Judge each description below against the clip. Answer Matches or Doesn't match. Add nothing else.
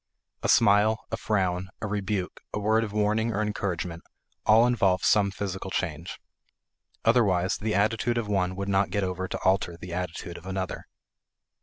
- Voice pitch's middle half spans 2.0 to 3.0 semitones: Matches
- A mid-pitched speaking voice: Doesn't match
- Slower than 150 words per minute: Doesn't match